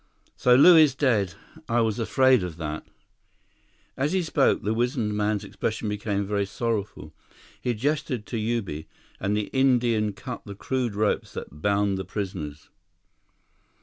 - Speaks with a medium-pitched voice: No, low, 110 Hz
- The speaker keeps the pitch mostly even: No, average, 3.7 semitones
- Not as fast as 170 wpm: Yes, average, 150 wpm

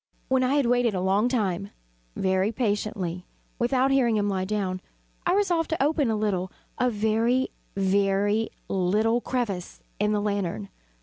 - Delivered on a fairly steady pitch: No, average, 4.1 semitones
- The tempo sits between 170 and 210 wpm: No, average, 150 wpm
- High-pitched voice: Yes, high, 210 Hz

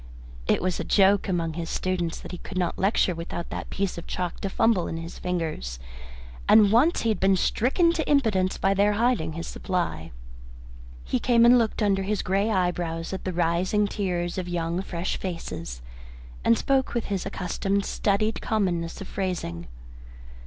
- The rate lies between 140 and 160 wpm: No, average, 175 wpm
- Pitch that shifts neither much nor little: Yes, average, 3.3 semitones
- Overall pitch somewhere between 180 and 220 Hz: Yes, medium, 185 Hz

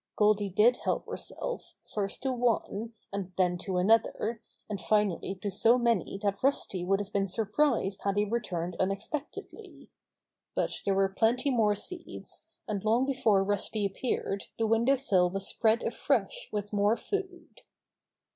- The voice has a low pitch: No, high, 210 Hz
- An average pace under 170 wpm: Yes, average, 155 wpm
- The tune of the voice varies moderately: Yes, average, 3.2 semitones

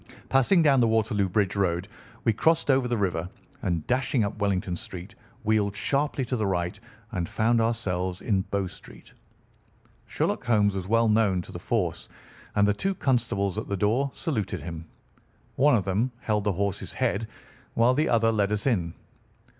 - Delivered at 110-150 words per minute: No, average, 175 wpm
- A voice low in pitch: Yes, low, 105 Hz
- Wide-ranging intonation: No, average, 3.8 semitones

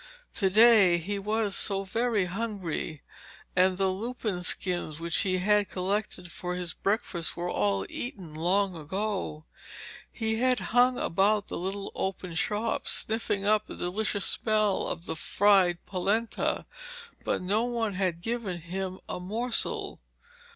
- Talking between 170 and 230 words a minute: No, slow, 135 wpm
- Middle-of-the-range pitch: No, high, 195 Hz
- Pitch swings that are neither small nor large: Yes, average, 3.2 semitones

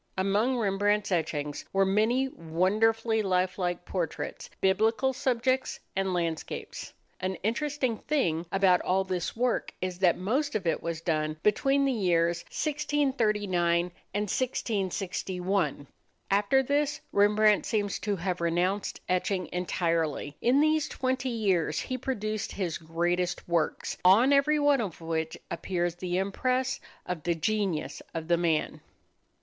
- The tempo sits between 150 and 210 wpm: No, slow, 135 wpm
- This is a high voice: Yes, high, 195 Hz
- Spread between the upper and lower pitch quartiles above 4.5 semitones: Yes, average, 5.1 semitones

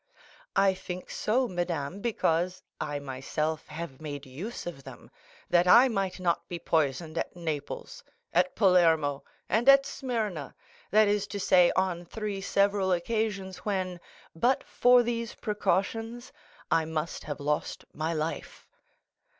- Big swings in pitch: No, average, 4.7 semitones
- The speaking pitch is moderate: Yes, medium, 180 Hz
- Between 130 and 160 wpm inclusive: Yes, slow, 135 wpm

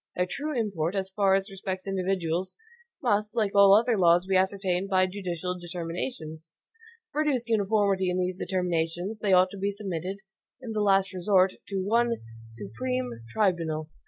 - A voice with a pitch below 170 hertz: No, high, 190 Hz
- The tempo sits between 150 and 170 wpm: Yes, average, 160 wpm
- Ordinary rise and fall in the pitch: No, narrow, 2.3 semitones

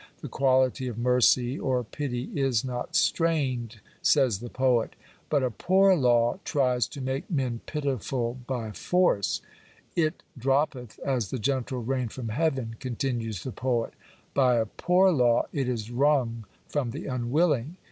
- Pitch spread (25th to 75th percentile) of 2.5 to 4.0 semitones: Yes, average, 2.8 semitones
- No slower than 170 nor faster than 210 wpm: No, average, 150 wpm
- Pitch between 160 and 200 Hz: No, low, 130 Hz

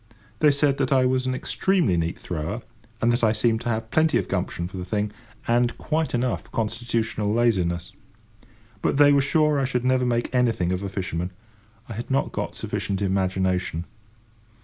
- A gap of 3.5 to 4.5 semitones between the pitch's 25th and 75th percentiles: No, average, 5.2 semitones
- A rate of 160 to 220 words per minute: Yes, average, 180 wpm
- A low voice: Yes, low, 115 Hz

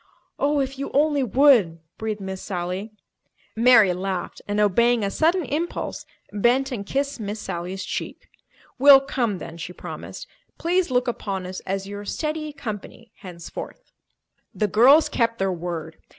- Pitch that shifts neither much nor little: No, wide, 6.2 semitones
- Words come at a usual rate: Yes, average, 150 wpm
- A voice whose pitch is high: Yes, high, 220 Hz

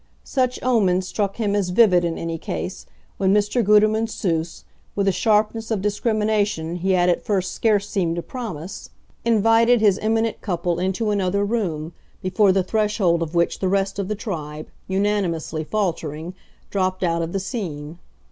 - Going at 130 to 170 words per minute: Yes, average, 165 wpm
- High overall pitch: Yes, high, 195 Hz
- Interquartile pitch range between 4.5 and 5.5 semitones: No, average, 3.7 semitones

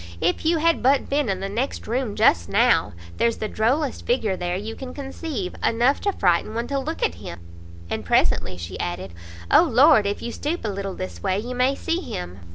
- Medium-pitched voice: No, high, 230 Hz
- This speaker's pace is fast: Yes, fast, 210 wpm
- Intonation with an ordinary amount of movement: No, wide, 6.9 semitones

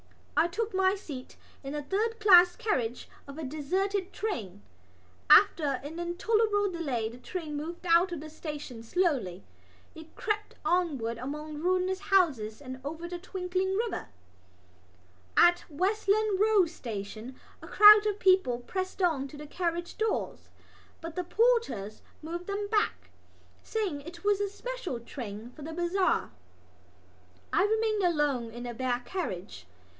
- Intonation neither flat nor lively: No, wide, 6.1 semitones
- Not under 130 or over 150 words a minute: Yes, average, 145 wpm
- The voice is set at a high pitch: Yes, very high, 345 Hz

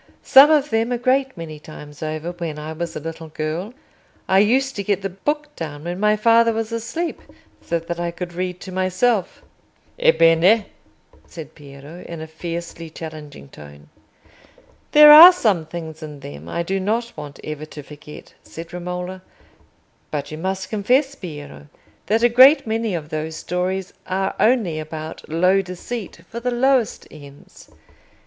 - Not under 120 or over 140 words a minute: No, average, 165 wpm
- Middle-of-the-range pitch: Yes, medium, 180 Hz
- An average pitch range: No, wide, 6.2 semitones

